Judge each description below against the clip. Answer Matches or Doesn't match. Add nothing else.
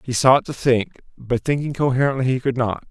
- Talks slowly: Doesn't match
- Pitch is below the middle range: Matches